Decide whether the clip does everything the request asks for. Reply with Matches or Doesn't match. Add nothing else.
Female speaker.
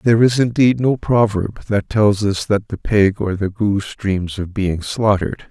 Doesn't match